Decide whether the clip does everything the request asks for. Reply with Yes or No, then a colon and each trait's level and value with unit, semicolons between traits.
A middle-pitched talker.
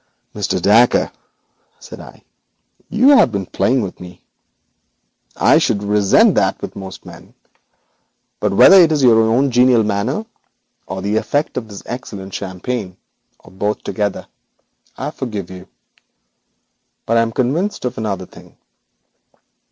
No: low, 110 Hz